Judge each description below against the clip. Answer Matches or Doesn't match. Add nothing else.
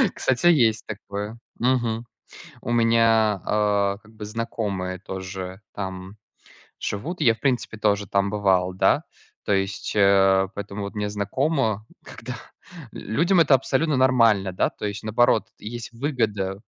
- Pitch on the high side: Doesn't match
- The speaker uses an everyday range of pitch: Matches